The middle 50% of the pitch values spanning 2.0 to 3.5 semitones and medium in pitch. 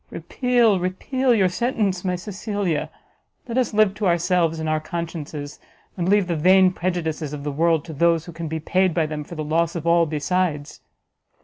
Yes: average, 3.1 semitones; medium, 170 Hz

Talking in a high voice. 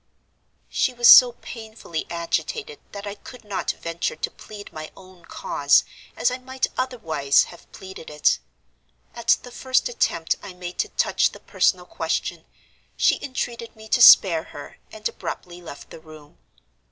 Yes: high, 200 Hz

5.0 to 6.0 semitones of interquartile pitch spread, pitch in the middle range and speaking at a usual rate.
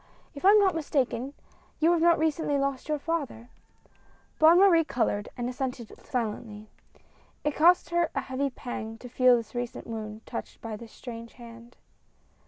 No: average, 5.3 semitones; very high, 255 Hz; average, 165 wpm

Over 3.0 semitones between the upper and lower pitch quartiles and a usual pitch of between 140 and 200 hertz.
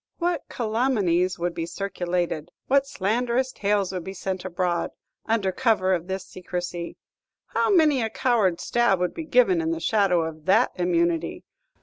Yes: average, 5.0 semitones; high, 190 Hz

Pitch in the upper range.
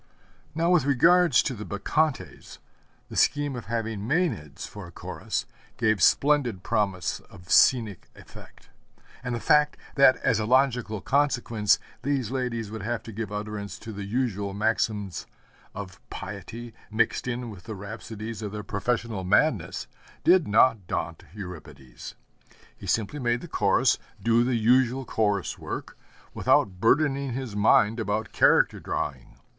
No: low, 115 Hz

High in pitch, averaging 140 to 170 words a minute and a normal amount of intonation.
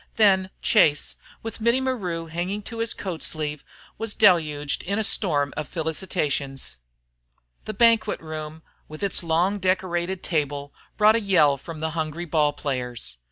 No: medium, 170 Hz; average, 150 wpm; average, 4.9 semitones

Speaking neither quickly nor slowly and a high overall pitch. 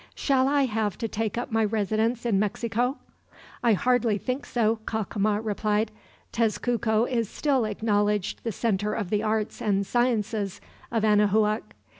Yes: average, 145 wpm; high, 220 Hz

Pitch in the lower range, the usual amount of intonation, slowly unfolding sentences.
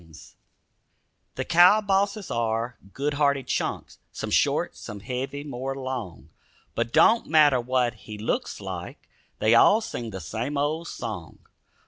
No: low, 130 Hz; average, 4.6 semitones; average, 145 wpm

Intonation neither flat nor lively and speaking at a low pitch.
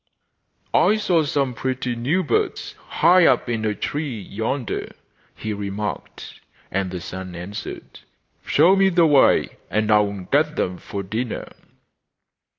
No: wide, 6.9 semitones; low, 115 Hz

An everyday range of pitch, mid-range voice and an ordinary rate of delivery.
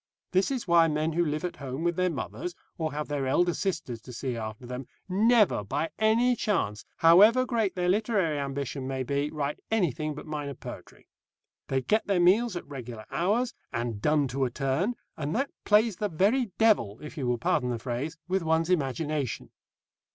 No: wide, 6.2 semitones; medium, 155 Hz; average, 190 wpm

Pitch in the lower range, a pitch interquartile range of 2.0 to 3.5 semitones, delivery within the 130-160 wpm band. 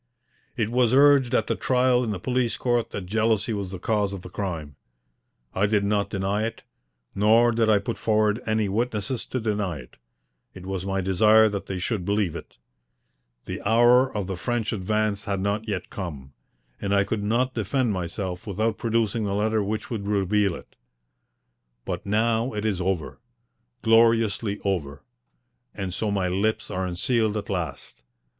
No: low, 105 Hz; average, 2.8 semitones; average, 170 wpm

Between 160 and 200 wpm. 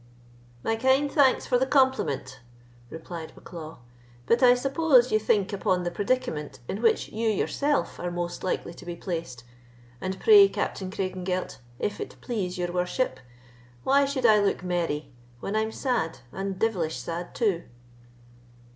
No: average, 150 wpm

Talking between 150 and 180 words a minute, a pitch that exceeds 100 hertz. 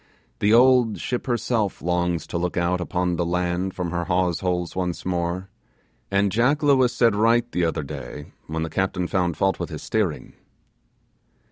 No: average, 170 wpm; very low, 90 Hz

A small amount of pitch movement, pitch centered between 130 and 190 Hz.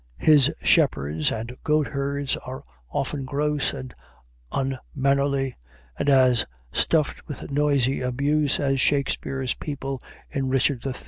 Yes: narrow, 1.6 semitones; low, 135 Hz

